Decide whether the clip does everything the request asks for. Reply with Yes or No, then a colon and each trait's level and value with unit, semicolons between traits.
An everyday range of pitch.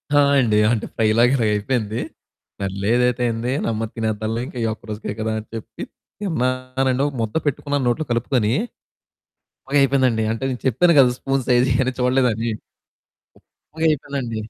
Yes: average, 3.1 semitones